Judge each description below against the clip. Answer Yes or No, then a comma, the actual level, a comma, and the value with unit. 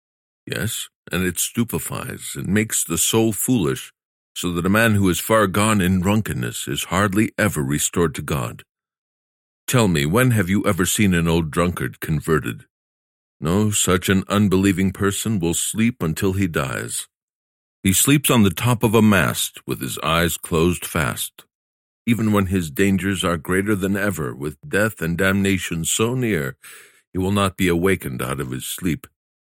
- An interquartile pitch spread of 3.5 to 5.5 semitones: Yes, average, 3.9 semitones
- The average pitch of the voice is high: No, very low, 95 Hz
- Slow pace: No, average, 165 wpm